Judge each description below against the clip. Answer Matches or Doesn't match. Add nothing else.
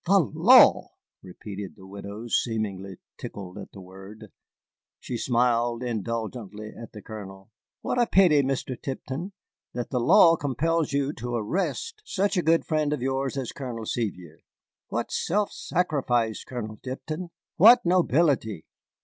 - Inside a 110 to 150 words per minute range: Matches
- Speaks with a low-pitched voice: Matches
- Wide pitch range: Matches